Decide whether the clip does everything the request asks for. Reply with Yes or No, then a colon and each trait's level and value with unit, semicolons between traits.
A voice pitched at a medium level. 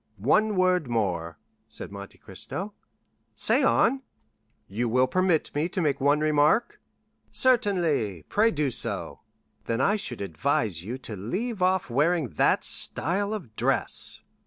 Yes: medium, 145 Hz